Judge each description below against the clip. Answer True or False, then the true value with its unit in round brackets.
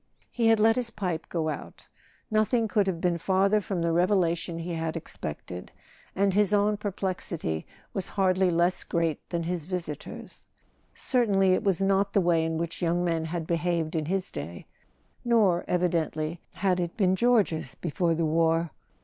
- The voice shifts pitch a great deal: False (2.9 semitones)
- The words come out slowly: False (165 wpm)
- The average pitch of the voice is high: False (175 Hz)